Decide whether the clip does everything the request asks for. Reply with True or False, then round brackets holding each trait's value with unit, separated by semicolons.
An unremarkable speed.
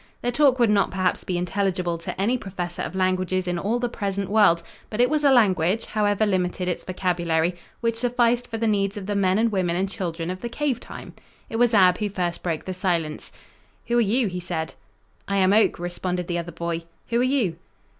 False (215 wpm)